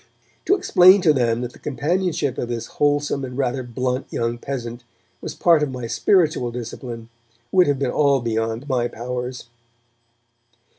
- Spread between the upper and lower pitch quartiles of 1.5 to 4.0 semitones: Yes, average, 3.5 semitones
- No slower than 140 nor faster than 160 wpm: Yes, average, 155 wpm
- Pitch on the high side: No, low, 130 Hz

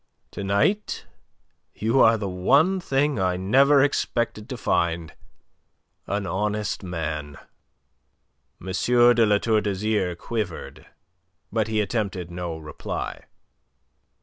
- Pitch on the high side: No, low, 105 Hz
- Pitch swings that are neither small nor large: Yes, average, 4.6 semitones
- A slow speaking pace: Yes, slow, 115 wpm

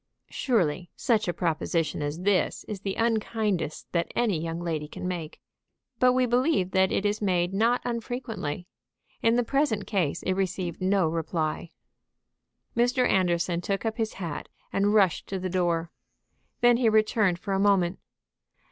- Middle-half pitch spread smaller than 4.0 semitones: No, average, 4.4 semitones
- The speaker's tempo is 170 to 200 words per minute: No, average, 155 wpm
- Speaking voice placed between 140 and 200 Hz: Yes, high, 190 Hz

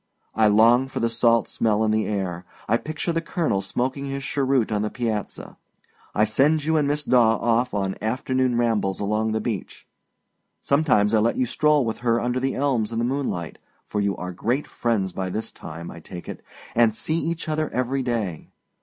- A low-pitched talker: Yes, low, 115 Hz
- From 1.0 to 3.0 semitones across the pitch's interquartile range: No, average, 4.0 semitones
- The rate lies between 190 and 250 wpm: Yes, average, 200 wpm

